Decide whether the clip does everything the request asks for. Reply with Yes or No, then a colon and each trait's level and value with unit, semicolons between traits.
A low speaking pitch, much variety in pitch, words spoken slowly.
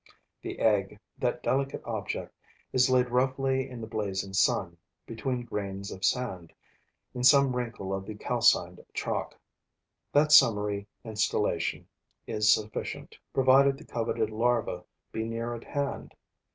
No: low, 115 Hz; average, 3.7 semitones; slow, 130 wpm